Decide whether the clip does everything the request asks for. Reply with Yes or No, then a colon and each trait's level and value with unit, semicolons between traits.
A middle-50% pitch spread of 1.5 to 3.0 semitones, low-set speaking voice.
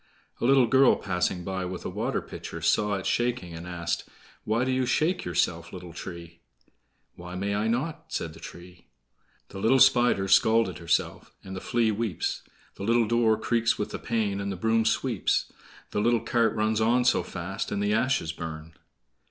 No: average, 4.7 semitones; low, 105 Hz